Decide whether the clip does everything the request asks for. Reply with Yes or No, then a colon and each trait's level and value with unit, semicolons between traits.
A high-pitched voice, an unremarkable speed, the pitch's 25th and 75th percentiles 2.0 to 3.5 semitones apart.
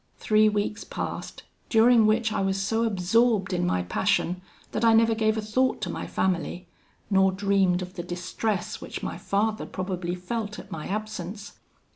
Yes: high, 205 Hz; average, 170 wpm; average, 3.2 semitones